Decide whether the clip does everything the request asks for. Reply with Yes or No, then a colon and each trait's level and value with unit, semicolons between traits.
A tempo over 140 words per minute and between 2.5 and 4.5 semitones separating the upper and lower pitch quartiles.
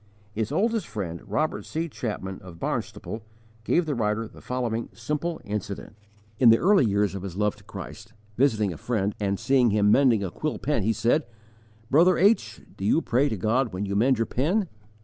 No: average, 190 wpm; average, 5.1 semitones